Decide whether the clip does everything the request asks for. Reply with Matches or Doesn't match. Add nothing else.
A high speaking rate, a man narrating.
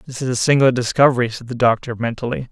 Matches